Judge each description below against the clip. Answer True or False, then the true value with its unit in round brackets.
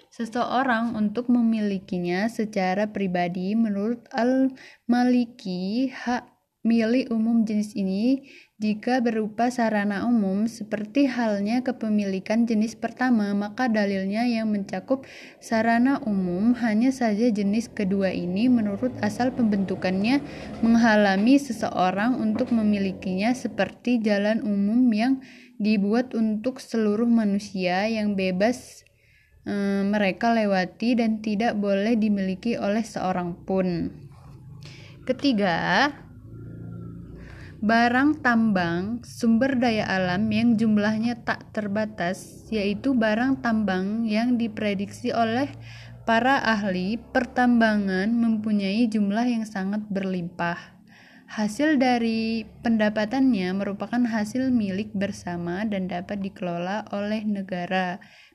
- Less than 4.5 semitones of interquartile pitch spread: True (3.2 semitones)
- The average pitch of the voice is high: True (215 Hz)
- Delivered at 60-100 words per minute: True (95 wpm)